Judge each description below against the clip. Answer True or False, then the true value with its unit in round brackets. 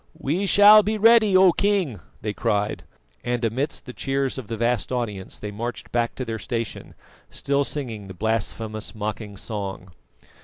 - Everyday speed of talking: True (160 wpm)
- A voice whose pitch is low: True (120 Hz)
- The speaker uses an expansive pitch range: False (5.0 semitones)